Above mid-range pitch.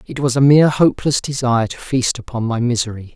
No: low, 125 Hz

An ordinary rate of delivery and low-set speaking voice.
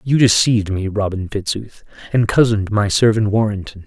Yes: average, 155 wpm; low, 105 Hz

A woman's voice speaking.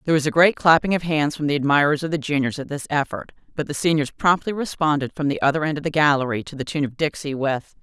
Yes: female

